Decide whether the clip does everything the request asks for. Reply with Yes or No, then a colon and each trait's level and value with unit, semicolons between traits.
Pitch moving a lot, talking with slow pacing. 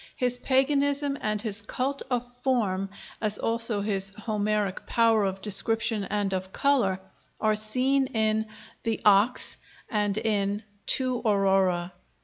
No: average, 3.7 semitones; slow, 125 wpm